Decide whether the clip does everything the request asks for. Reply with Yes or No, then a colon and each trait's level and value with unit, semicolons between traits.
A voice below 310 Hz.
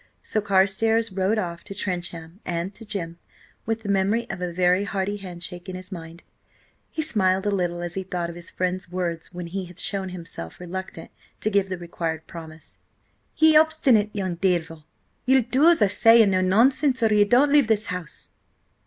Yes: high, 190 Hz